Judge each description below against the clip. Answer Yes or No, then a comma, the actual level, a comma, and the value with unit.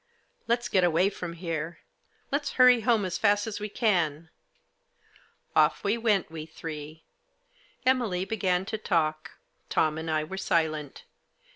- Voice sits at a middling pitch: Yes, medium, 180 Hz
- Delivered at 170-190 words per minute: No, average, 145 wpm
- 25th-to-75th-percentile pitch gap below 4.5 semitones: No, average, 5.0 semitones